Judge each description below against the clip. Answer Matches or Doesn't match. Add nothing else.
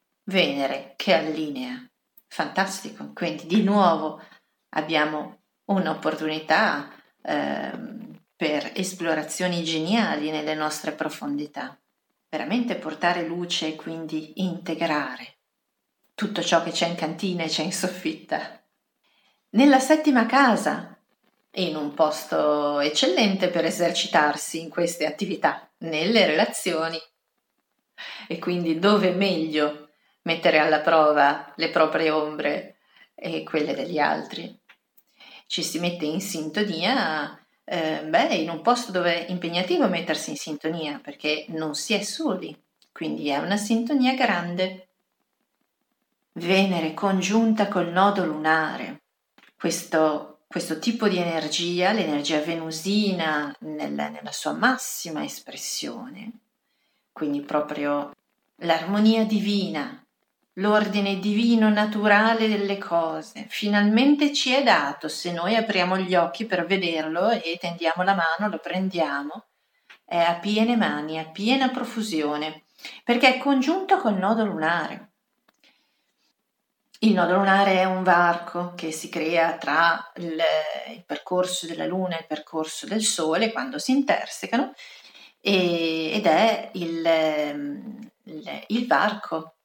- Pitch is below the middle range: Doesn't match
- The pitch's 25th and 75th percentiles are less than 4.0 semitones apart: Doesn't match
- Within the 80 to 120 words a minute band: Matches